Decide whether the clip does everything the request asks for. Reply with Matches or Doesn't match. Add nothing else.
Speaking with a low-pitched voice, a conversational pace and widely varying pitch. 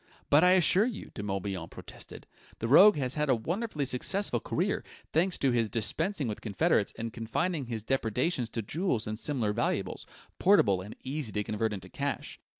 Matches